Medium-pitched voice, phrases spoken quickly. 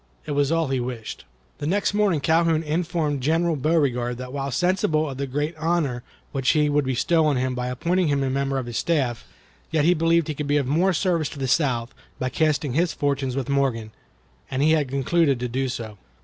Yes: medium, 145 Hz; fast, 215 wpm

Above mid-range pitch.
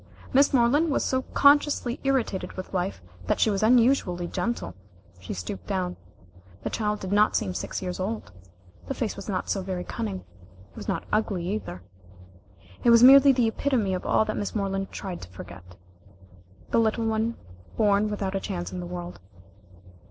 Yes: high, 205 Hz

